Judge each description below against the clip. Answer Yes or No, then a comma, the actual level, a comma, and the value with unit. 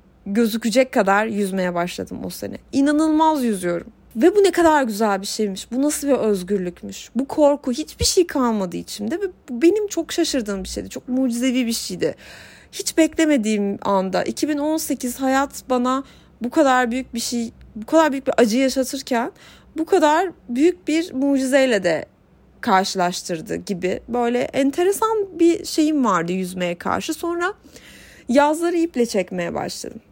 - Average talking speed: No, fast, 145 wpm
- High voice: Yes, very high, 260 Hz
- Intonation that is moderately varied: No, wide, 6.8 semitones